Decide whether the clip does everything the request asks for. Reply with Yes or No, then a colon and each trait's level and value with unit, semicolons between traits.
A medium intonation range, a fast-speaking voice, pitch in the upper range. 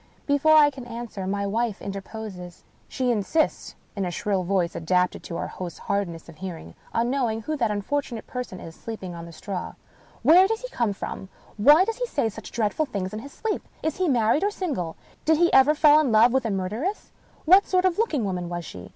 No: wide, 7.8 semitones; fast, 215 wpm; high, 225 Hz